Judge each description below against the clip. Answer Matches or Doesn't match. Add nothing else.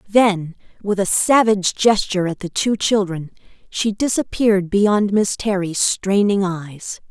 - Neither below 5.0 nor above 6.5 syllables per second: Doesn't match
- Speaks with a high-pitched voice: Matches